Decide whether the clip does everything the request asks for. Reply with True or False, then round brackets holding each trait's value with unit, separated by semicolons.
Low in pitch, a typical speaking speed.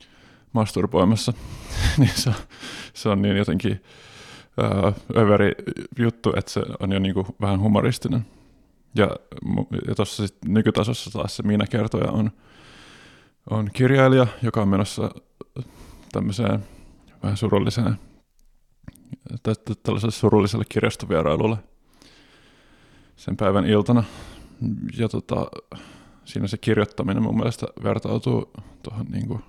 True (110 Hz; 105 wpm)